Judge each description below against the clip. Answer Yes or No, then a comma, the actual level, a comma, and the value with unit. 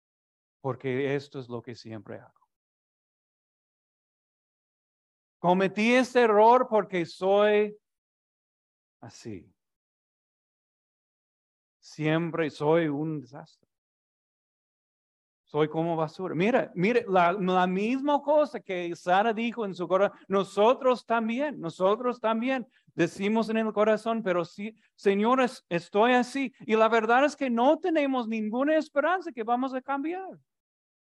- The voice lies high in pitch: Yes, high, 210 Hz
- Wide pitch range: Yes, wide, 6.3 semitones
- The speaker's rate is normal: No, slow, 110 wpm